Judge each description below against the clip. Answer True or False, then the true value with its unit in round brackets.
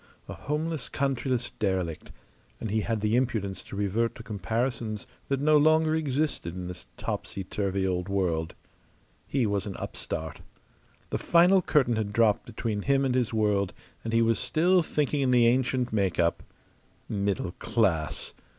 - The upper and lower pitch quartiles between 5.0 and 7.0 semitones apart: True (5.3 semitones)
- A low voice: True (115 Hz)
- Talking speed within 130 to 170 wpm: True (160 wpm)